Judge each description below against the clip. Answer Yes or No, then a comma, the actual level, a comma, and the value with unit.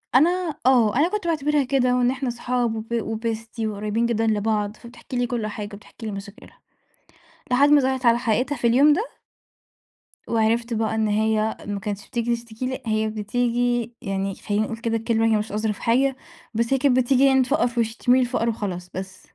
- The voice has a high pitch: Yes, high, 230 Hz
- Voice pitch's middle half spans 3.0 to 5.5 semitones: No, narrow, 2.6 semitones